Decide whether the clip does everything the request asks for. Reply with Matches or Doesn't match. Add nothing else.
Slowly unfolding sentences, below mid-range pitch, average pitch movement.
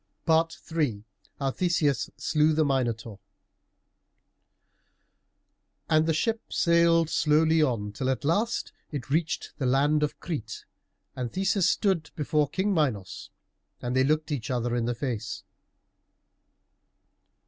Doesn't match